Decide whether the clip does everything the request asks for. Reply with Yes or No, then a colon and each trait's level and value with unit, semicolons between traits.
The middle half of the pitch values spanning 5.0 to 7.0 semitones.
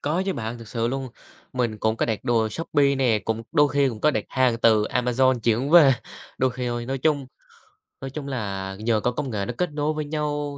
No: average, 4.1 semitones